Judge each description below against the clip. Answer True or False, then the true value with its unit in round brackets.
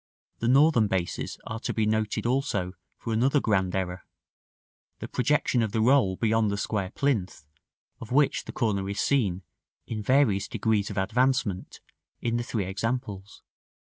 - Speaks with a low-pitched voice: True (110 Hz)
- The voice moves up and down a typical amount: True (4.2 semitones)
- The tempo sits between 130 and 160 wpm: True (155 wpm)